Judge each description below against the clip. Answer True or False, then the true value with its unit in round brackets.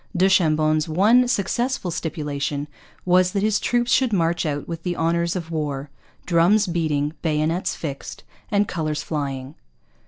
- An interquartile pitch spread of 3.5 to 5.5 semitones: True (3.8 semitones)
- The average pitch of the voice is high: False (165 Hz)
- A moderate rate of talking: True (145 wpm)